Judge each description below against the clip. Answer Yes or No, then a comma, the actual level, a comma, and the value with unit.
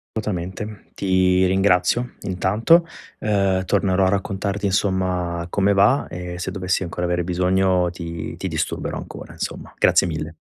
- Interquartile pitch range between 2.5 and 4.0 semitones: No, narrow, 2.0 semitones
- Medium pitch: No, very low, 95 Hz